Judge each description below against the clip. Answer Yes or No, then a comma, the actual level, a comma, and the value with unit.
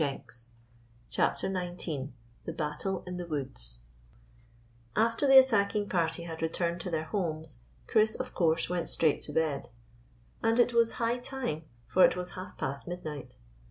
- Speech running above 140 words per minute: Yes, average, 160 wpm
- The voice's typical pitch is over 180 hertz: No, medium, 175 Hz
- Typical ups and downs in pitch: Yes, average, 4.8 semitones